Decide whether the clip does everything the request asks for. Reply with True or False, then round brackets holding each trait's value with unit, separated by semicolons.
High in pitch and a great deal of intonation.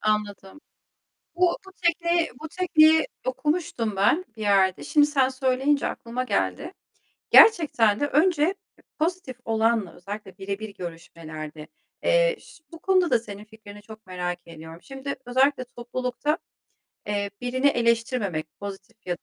True (235 Hz; 6.7 semitones)